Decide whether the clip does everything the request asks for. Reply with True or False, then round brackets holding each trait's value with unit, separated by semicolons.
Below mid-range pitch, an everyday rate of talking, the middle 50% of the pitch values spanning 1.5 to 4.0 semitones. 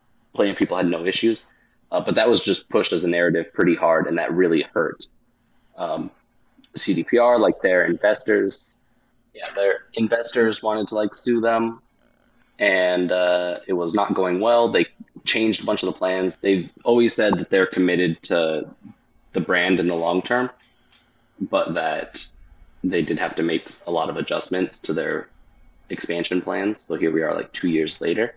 False (105 Hz; 180 wpm; 4.6 semitones)